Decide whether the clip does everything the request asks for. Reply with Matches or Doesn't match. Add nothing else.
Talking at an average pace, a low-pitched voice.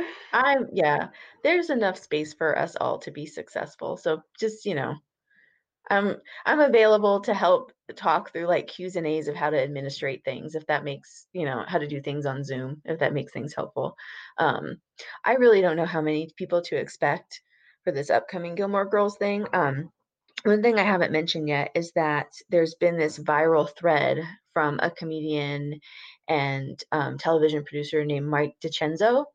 Doesn't match